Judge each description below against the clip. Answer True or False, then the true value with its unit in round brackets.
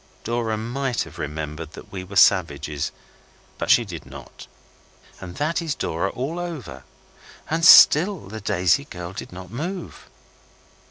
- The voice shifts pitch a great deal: True (9.0 semitones)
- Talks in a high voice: False (100 Hz)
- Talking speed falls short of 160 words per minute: True (145 wpm)